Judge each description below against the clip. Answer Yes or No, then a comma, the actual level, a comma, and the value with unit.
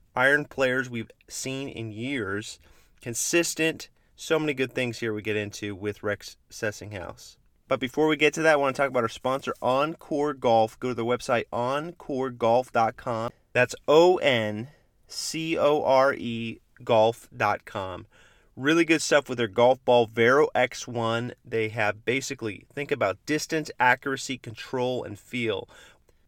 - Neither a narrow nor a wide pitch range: Yes, average, 3.9 semitones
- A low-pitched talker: Yes, low, 125 Hz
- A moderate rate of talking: Yes, average, 150 wpm